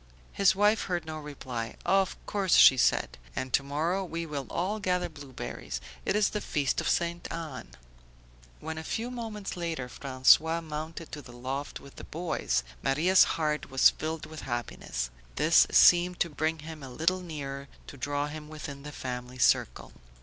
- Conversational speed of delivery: Yes, average, 170 wpm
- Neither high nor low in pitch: Yes, medium, 155 Hz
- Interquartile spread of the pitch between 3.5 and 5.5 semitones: Yes, average, 4.1 semitones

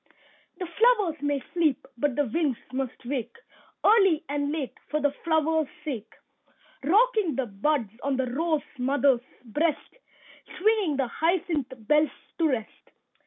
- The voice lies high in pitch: Yes, very high, 295 Hz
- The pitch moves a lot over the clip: No, average, 3.9 semitones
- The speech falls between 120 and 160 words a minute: Yes, slow, 135 wpm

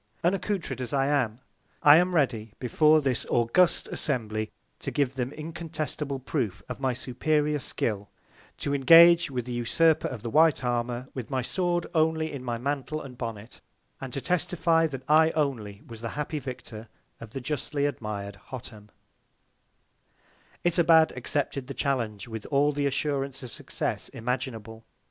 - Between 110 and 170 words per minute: Yes, average, 155 wpm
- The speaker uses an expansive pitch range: No, average, 4.5 semitones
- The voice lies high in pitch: No, low, 135 Hz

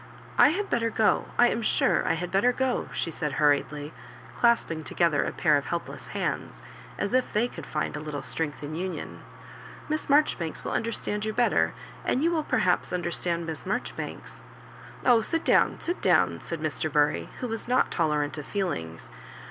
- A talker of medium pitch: Yes, medium, 175 Hz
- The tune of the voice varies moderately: No, wide, 7.7 semitones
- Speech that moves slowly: No, average, 190 wpm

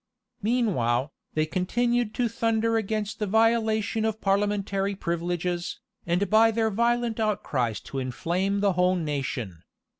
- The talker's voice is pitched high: Yes, high, 200 Hz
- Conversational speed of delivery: No, slow, 125 wpm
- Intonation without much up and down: No, average, 4.4 semitones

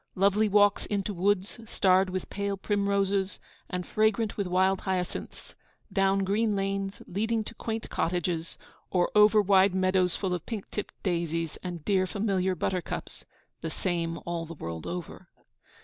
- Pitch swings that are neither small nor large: No, narrow, 2.1 semitones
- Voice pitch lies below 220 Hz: Yes, high, 190 Hz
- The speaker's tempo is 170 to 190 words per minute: No, average, 150 wpm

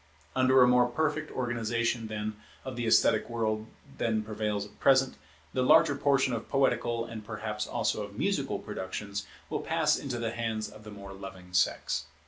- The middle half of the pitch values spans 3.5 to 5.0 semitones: No, average, 2.8 semitones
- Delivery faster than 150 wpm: Yes, average, 170 wpm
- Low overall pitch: Yes, low, 115 Hz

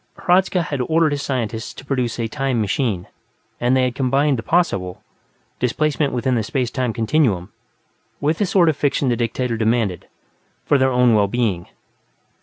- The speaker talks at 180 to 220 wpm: No, average, 170 wpm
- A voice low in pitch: Yes, low, 125 Hz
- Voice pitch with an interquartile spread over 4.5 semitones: No, average, 4.0 semitones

